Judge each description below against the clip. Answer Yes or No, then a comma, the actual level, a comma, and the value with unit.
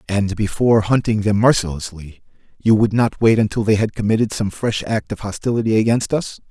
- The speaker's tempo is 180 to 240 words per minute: Yes, average, 185 wpm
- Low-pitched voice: Yes, low, 110 Hz